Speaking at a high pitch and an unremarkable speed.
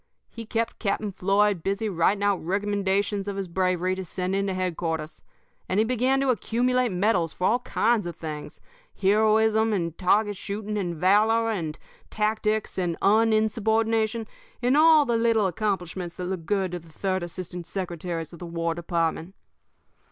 Yes: high, 200 Hz; average, 160 wpm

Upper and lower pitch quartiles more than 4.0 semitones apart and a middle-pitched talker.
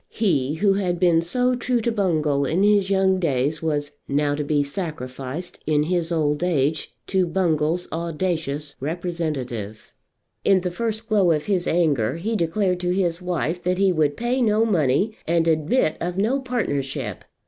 Yes: average, 4.4 semitones; medium, 170 Hz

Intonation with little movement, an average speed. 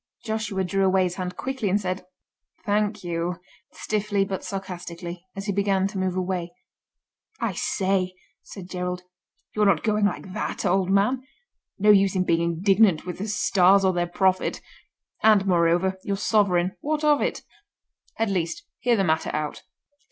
Yes: narrow, 2.2 semitones; average, 155 wpm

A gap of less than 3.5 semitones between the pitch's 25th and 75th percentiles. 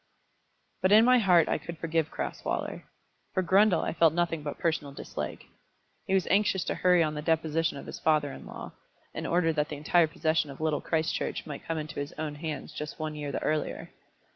Yes: narrow, 2.4 semitones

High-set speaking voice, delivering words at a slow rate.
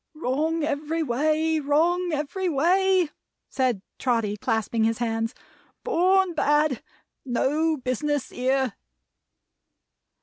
Yes: very high, 290 Hz; slow, 95 wpm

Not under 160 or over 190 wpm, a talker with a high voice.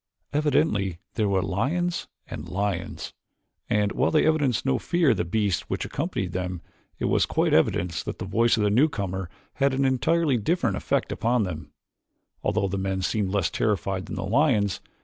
No: average, 175 wpm; low, 105 Hz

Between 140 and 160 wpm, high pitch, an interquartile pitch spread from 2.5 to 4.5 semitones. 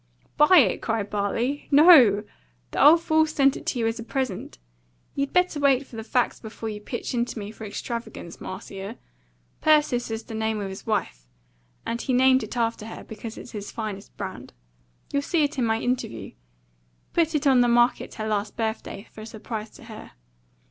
No: average, 190 wpm; high, 230 Hz; average, 4.1 semitones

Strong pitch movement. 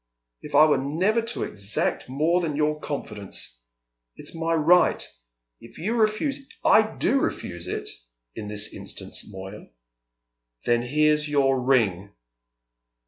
Yes: wide, 7.6 semitones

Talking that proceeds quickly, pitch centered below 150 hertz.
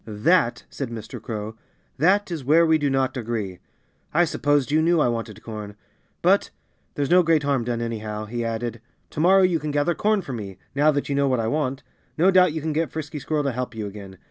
Yes: fast, 220 wpm; medium, 140 Hz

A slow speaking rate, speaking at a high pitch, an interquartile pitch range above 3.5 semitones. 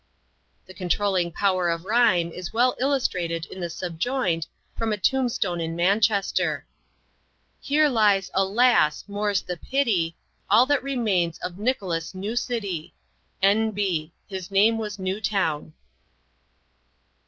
Yes: slow, 120 wpm; high, 195 Hz; average, 4.4 semitones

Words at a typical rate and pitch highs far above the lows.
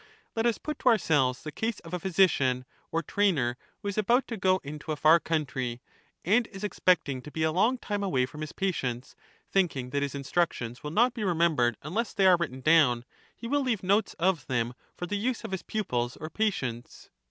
No: fast, 215 wpm; wide, 7.3 semitones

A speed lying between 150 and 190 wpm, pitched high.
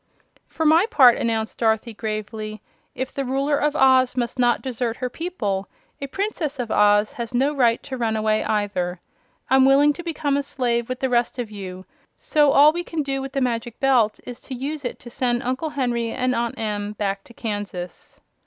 No: average, 200 wpm; high, 245 Hz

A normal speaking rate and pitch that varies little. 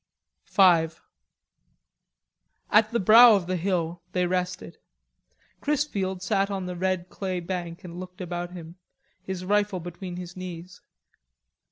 No: slow, 130 wpm; narrow, 1.7 semitones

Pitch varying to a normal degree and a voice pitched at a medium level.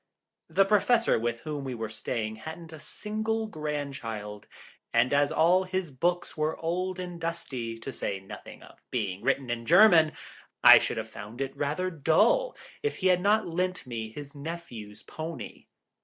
No: wide, 7.2 semitones; medium, 155 Hz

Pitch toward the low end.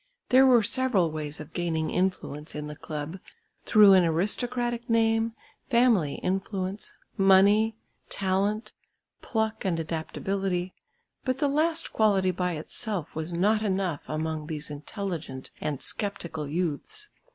No: high, 190 Hz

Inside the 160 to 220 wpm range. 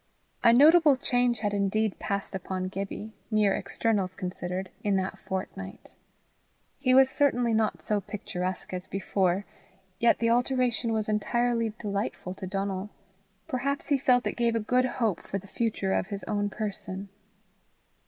No: average, 150 wpm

